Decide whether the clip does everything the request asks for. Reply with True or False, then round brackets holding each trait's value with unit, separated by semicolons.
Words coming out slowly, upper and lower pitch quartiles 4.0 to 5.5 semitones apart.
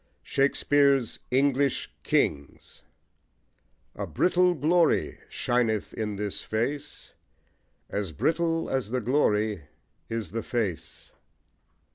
True (90 wpm; 5.1 semitones)